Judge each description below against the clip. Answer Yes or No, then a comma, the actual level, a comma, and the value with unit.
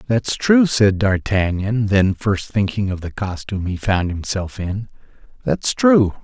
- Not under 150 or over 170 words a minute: Yes, average, 155 wpm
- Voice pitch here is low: Yes, low, 105 Hz